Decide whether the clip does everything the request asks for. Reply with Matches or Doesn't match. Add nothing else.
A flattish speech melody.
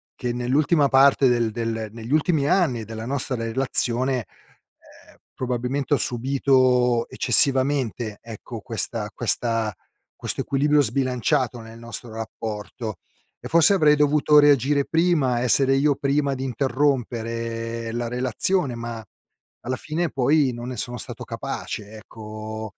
Doesn't match